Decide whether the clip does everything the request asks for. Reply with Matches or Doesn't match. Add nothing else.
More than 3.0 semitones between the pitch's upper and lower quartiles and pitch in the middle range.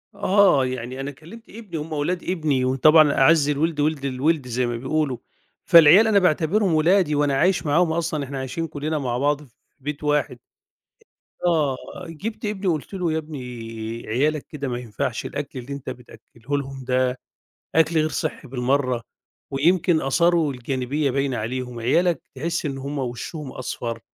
Matches